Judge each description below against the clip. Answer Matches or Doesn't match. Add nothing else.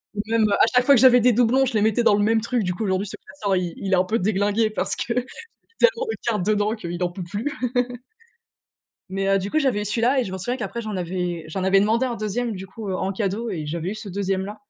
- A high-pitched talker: Matches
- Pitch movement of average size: Matches